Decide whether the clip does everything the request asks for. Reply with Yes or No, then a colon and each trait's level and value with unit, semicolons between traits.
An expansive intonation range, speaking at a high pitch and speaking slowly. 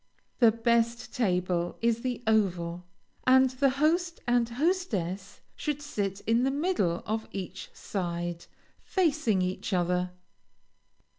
Yes: wide, 6.3 semitones; high, 225 Hz; slow, 120 wpm